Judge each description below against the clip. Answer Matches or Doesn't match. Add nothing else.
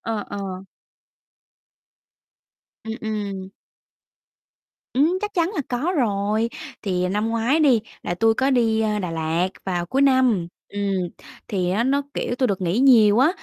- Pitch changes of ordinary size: Matches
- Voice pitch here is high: Matches